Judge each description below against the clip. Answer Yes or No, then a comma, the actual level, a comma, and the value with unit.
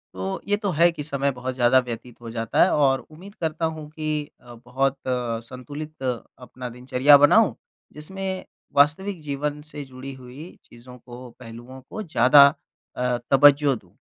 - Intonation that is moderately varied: Yes, average, 3.2 semitones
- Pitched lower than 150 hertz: Yes, low, 135 Hz